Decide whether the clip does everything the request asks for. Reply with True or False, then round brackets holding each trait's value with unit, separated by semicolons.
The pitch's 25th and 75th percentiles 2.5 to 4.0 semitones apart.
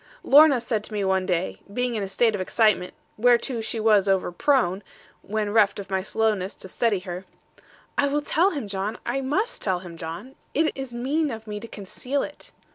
False (5.1 semitones)